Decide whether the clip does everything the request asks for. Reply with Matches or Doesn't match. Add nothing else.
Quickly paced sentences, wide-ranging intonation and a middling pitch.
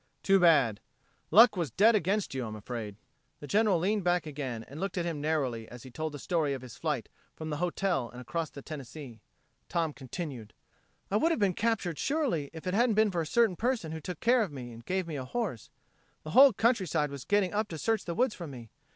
Matches